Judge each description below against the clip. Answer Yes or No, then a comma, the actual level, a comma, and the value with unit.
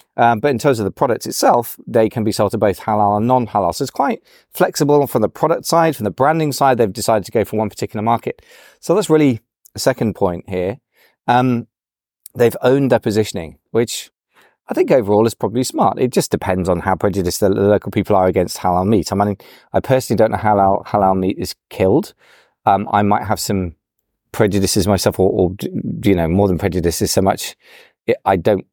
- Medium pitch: No, low, 105 Hz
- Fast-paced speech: Yes, fast, 210 wpm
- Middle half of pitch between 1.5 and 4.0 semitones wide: Yes, average, 3.2 semitones